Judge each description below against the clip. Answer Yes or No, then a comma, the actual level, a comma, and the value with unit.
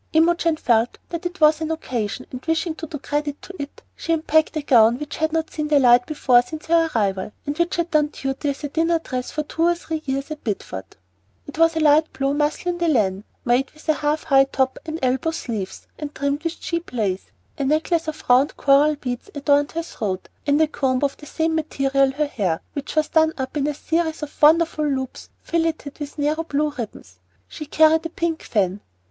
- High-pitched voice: Yes, very high, 295 Hz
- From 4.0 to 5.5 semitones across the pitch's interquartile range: No, average, 3.3 semitones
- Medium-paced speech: No, fast, 215 wpm